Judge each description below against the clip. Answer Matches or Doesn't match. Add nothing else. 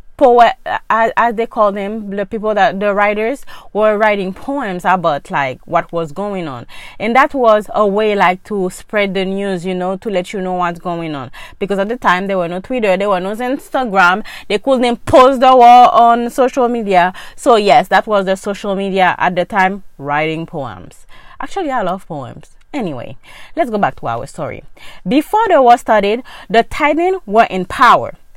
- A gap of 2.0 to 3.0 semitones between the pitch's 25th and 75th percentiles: Doesn't match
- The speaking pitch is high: Matches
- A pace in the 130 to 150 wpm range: Doesn't match